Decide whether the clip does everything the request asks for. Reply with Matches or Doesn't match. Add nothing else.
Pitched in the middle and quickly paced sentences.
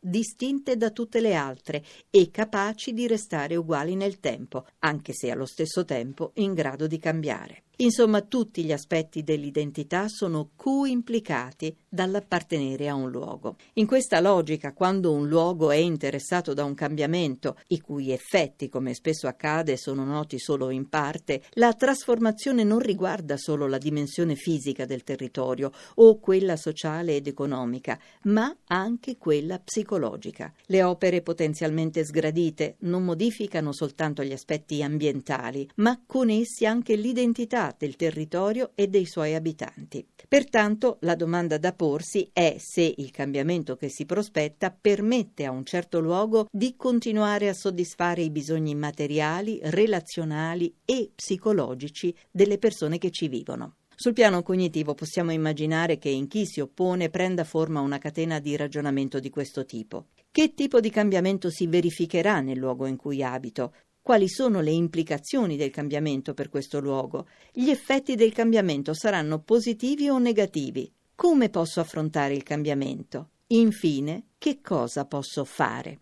Doesn't match